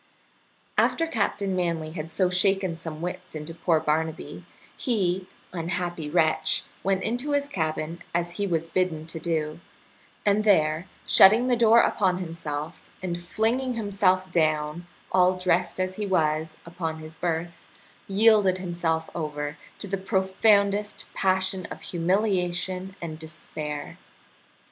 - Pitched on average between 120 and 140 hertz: No, medium, 180 Hz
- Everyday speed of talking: No, slow, 130 wpm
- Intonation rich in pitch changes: No, average, 3.1 semitones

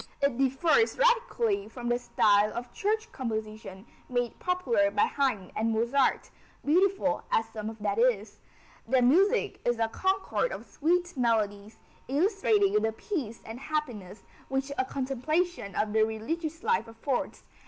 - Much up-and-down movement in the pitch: Yes, wide, 7.8 semitones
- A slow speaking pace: No, average, 145 wpm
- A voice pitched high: Yes, very high, 255 Hz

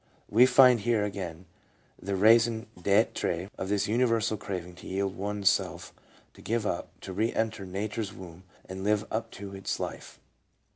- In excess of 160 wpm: No, average, 155 wpm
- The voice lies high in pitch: No, low, 105 Hz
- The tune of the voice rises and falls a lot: No, average, 2.9 semitones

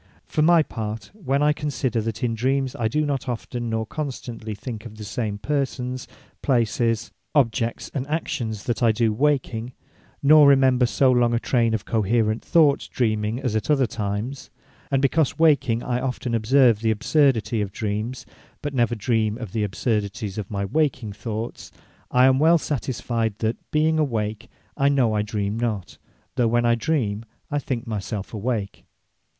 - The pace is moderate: Yes, average, 170 wpm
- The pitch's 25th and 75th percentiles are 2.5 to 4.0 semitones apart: Yes, average, 3.7 semitones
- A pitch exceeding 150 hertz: No, low, 120 Hz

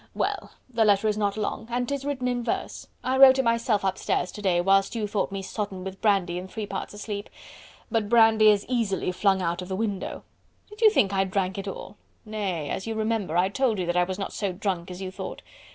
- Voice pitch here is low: No, high, 205 Hz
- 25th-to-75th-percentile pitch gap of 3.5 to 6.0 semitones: No, average, 3.0 semitones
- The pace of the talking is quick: Yes, fast, 230 wpm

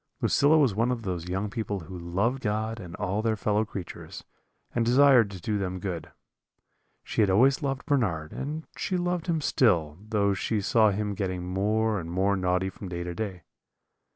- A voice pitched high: No, low, 105 Hz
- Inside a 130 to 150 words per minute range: No, average, 185 wpm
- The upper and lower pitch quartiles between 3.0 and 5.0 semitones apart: Yes, average, 4.1 semitones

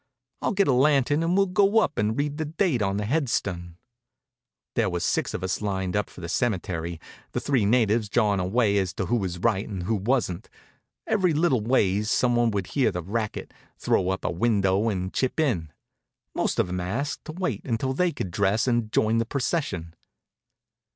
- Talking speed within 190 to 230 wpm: Yes, average, 200 wpm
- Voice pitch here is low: Yes, low, 110 Hz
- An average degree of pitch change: No, wide, 6.1 semitones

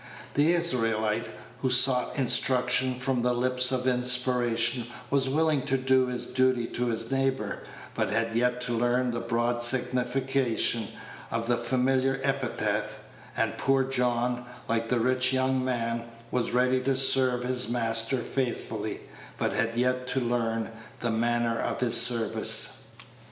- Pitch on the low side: Yes, low, 125 Hz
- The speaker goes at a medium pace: Yes, average, 145 wpm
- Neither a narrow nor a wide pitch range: No, narrow, 1.7 semitones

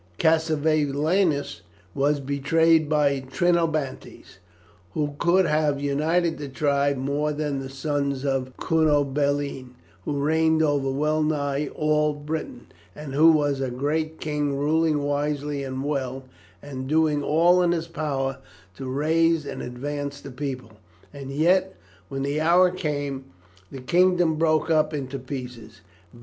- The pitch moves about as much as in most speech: No, narrow, 2.3 semitones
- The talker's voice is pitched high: No, medium, 145 Hz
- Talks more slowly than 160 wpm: Yes, slow, 135 wpm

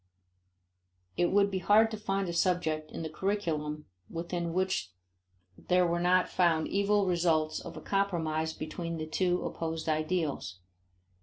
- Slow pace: No, average, 145 wpm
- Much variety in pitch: No, average, 3.0 semitones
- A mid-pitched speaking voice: Yes, medium, 170 Hz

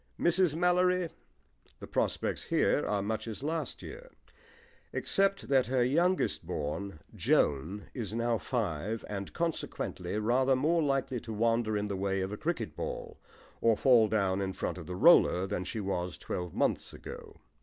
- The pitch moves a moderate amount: No, wide, 8.2 semitones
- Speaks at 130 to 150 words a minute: No, average, 160 wpm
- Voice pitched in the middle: No, low, 115 Hz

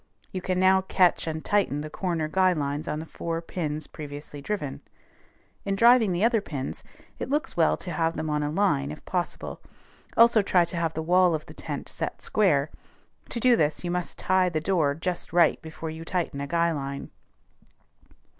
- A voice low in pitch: No, medium, 170 Hz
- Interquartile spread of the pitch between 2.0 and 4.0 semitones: Yes, average, 3.5 semitones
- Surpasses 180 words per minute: Yes, average, 190 wpm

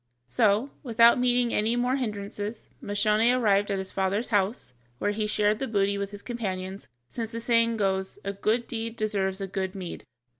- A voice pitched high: Yes, high, 210 Hz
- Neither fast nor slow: Yes, average, 180 wpm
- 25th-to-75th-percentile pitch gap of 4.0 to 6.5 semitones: No, average, 2.8 semitones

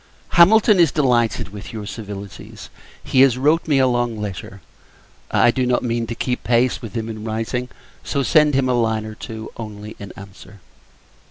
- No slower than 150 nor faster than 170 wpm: No, average, 180 wpm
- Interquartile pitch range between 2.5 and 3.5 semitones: Yes, average, 3.2 semitones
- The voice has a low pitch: Yes, low, 115 Hz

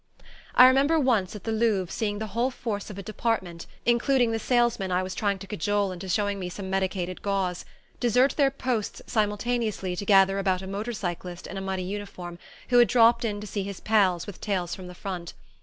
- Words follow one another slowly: No, fast, 205 wpm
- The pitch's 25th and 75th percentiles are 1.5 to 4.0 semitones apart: Yes, average, 3.5 semitones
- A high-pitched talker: Yes, high, 205 Hz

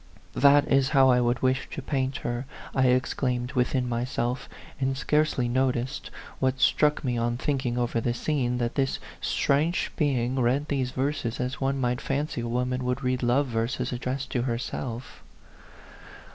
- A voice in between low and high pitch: No, low, 130 Hz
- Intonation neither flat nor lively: No, narrow, 1.8 semitones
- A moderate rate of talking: Yes, average, 175 wpm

